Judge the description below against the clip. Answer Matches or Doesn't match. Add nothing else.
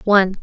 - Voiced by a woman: Matches